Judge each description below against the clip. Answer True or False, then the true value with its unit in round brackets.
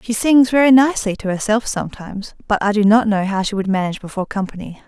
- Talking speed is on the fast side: True (220 wpm)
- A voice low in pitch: False (210 Hz)